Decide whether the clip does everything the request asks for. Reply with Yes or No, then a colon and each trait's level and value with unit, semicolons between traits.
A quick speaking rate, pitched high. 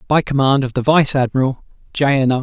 No: fast, 225 wpm; low, 135 Hz